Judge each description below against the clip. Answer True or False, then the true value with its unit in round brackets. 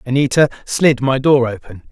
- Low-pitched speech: True (130 Hz)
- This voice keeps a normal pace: True (155 wpm)